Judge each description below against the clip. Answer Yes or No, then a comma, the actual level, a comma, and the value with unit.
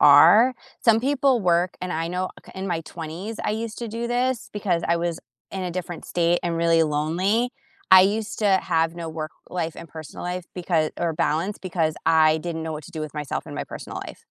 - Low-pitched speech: No, medium, 175 Hz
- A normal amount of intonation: Yes, average, 3.7 semitones